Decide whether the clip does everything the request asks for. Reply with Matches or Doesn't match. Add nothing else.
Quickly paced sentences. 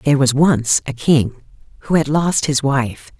Doesn't match